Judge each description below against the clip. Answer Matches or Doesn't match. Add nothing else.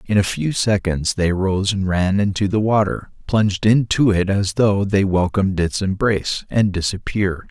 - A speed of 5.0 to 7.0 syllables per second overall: Doesn't match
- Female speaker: Doesn't match